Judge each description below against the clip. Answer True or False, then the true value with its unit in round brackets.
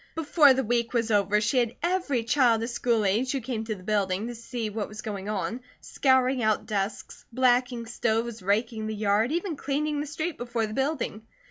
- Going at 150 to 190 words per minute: False (200 wpm)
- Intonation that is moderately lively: True (3.4 semitones)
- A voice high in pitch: True (235 Hz)